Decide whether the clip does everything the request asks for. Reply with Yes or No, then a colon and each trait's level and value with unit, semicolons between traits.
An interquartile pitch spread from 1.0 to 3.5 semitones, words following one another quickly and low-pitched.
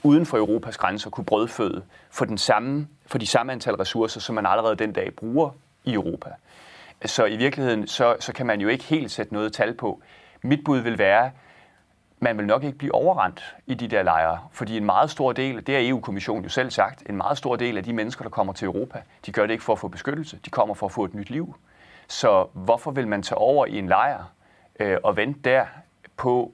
No: average, 4.1 semitones; fast, 235 wpm; low, 125 Hz